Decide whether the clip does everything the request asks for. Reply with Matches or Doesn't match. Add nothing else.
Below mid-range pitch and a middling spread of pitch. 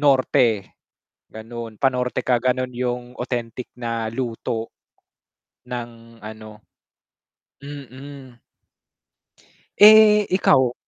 Doesn't match